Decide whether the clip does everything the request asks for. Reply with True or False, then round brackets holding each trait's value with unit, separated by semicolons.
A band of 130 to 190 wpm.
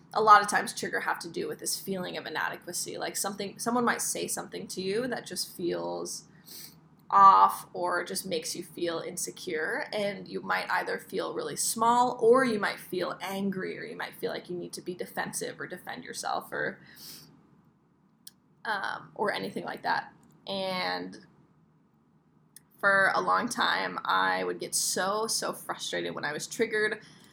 True (170 wpm)